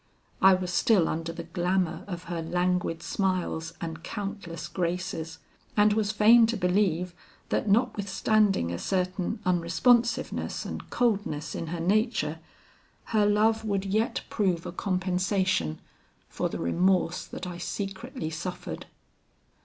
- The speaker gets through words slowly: Yes, slow, 130 wpm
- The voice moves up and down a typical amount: Yes, average, 3.3 semitones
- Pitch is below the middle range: No, medium, 185 Hz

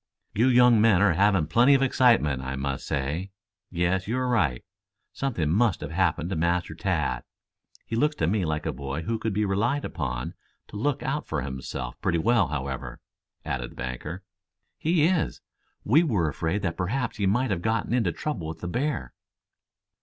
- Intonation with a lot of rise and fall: Yes, wide, 7.4 semitones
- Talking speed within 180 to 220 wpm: Yes, average, 185 wpm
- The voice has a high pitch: No, very low, 95 Hz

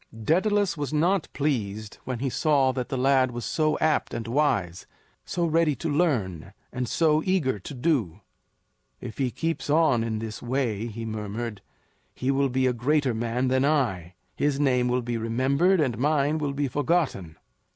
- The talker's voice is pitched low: Yes, low, 130 Hz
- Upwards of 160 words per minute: Yes, average, 170 wpm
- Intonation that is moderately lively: Yes, average, 4.7 semitones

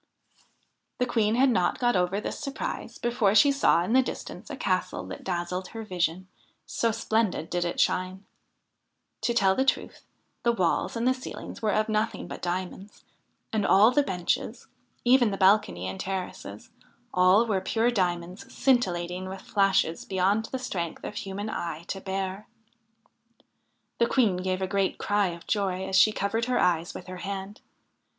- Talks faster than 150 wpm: Yes, average, 170 wpm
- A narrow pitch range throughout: No, average, 3.7 semitones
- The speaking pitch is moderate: No, high, 195 Hz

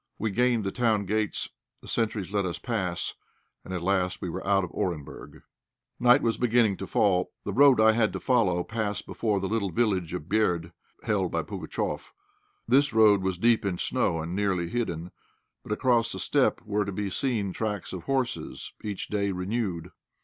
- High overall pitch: No, low, 100 Hz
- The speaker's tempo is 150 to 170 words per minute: No, average, 185 wpm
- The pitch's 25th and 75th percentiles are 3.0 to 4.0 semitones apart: Yes, average, 3.6 semitones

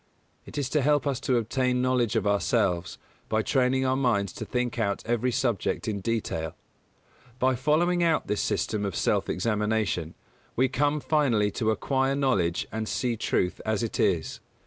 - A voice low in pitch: Yes, low, 120 Hz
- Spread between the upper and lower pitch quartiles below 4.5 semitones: Yes, average, 3.9 semitones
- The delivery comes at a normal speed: Yes, average, 170 wpm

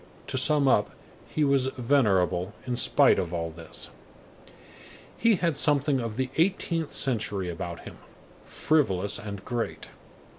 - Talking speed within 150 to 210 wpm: No, slow, 135 wpm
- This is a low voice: Yes, low, 125 Hz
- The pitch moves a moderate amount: No, wide, 7.2 semitones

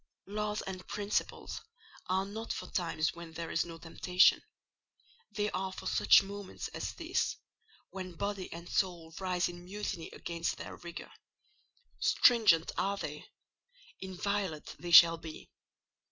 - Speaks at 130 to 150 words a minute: Yes, average, 140 wpm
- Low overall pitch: No, medium, 185 Hz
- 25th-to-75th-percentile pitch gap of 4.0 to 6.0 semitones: No, average, 3.0 semitones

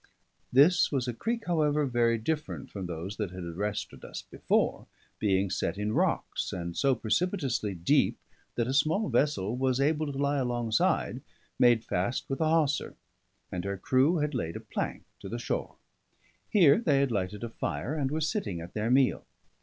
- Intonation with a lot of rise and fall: Yes, wide, 6.3 semitones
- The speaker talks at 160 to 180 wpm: Yes, average, 175 wpm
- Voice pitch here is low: Yes, low, 125 Hz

